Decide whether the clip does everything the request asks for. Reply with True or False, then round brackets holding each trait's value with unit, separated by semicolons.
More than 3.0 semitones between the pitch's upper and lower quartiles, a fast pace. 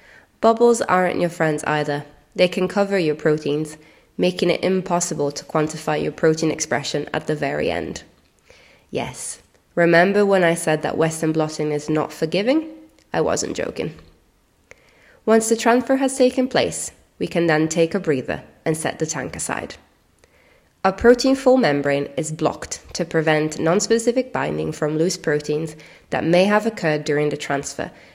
False (4.1 semitones; 155 wpm)